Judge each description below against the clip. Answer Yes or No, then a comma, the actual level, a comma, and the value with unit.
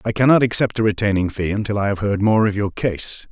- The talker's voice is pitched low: Yes, low, 105 Hz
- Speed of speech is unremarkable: No, fast, 270 wpm